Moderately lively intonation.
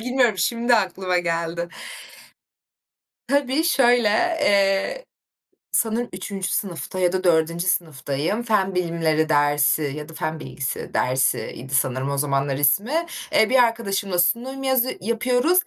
No: wide, 7.1 semitones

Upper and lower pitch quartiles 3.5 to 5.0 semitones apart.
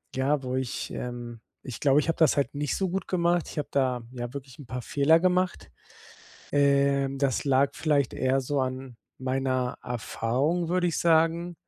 Yes: average, 3.8 semitones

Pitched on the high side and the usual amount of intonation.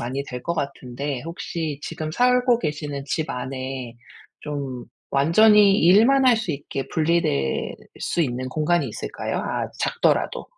No: medium, 150 Hz; average, 4.8 semitones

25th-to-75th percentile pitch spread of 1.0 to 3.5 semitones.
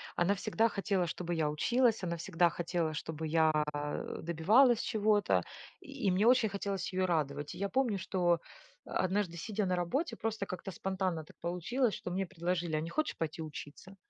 No: average, 3.9 semitones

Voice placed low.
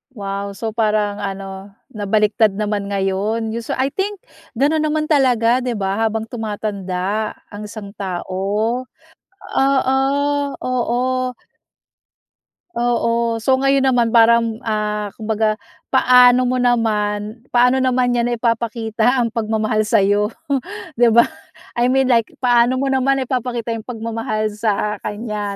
No: high, 225 Hz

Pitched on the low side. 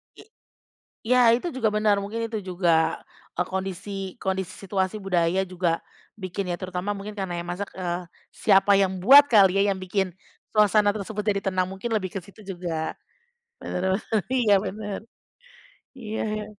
No: high, 195 Hz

